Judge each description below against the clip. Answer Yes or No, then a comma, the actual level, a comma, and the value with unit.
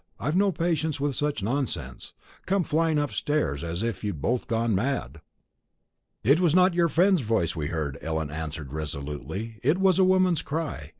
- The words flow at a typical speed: Yes, average, 170 wpm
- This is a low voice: Yes, low, 130 Hz